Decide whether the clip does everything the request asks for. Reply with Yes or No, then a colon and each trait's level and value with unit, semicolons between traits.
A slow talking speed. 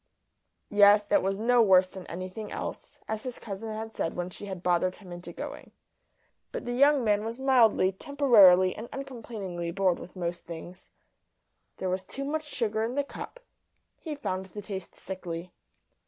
No: average, 170 wpm